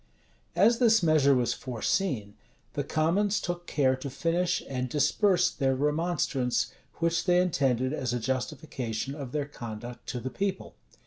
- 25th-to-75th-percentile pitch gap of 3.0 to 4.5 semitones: No, wide, 5.4 semitones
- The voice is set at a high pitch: No, medium, 140 Hz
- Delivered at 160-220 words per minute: No, average, 145 wpm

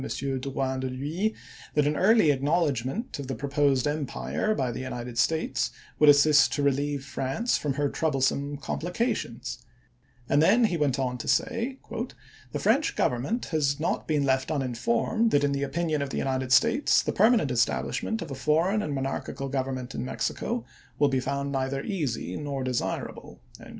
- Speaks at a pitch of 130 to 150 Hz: Yes, medium, 140 Hz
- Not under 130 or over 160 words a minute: No, average, 170 wpm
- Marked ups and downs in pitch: No, average, 3.2 semitones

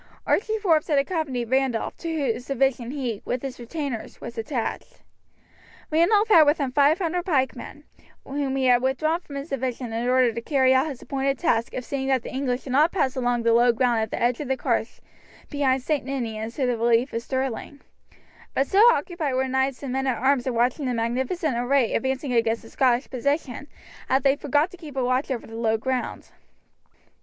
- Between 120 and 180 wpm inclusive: No, average, 200 wpm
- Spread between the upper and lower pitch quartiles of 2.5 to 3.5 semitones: Yes, average, 2.8 semitones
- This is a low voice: No, very high, 265 Hz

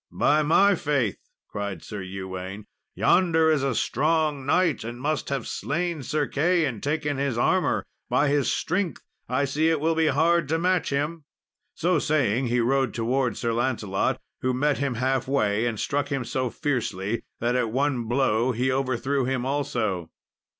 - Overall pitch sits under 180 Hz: Yes, low, 135 Hz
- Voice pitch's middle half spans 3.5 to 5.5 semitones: Yes, average, 4.3 semitones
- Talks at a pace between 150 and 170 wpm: Yes, average, 165 wpm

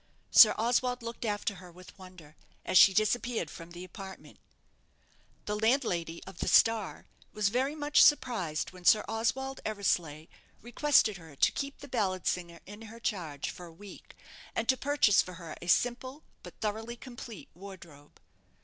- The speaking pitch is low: No, high, 210 Hz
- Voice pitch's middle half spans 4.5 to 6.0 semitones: Yes, average, 5.2 semitones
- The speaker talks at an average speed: Yes, average, 160 wpm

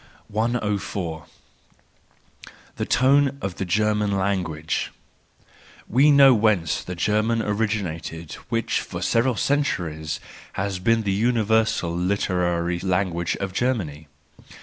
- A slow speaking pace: Yes, slow, 105 wpm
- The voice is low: Yes, low, 100 Hz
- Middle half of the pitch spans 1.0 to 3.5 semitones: No, average, 4.5 semitones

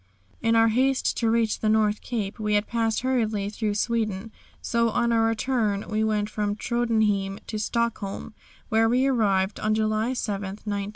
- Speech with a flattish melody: Yes, narrow, 1.9 semitones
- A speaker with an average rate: Yes, average, 170 wpm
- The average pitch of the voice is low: No, high, 220 Hz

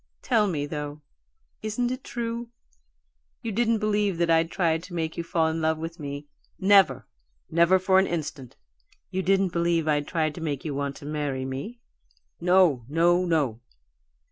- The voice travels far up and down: No, average, 4.2 semitones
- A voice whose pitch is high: No, medium, 165 Hz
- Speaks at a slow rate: No, average, 175 wpm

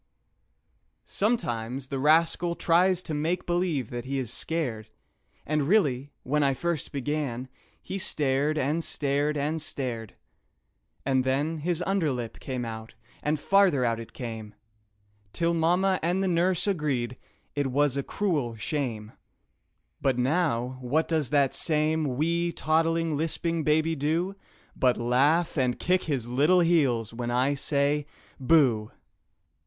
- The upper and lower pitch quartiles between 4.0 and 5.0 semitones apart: Yes, average, 4.6 semitones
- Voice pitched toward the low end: No, medium, 145 Hz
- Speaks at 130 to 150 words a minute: Yes, average, 140 wpm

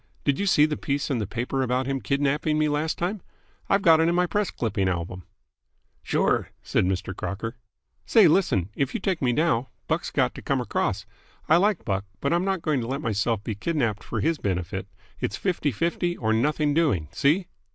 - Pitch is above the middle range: No, medium, 140 Hz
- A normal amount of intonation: No, wide, 7.1 semitones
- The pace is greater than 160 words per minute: Yes, fast, 205 wpm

